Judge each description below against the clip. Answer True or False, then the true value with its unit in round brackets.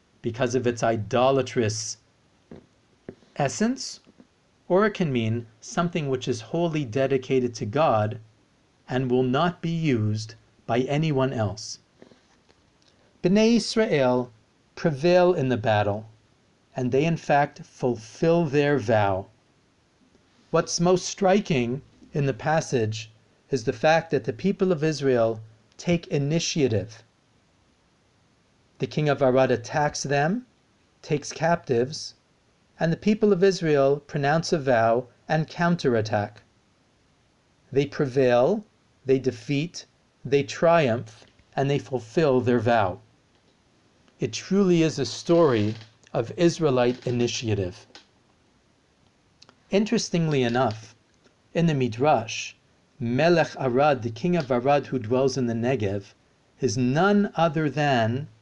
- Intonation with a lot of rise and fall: True (5.8 semitones)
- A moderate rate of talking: False (115 wpm)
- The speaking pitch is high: False (130 Hz)